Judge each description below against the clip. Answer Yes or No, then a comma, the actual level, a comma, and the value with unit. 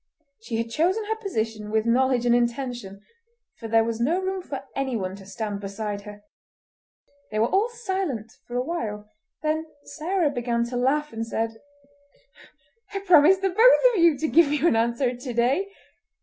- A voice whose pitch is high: Yes, very high, 250 Hz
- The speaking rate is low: No, average, 175 wpm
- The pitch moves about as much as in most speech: No, wide, 7.2 semitones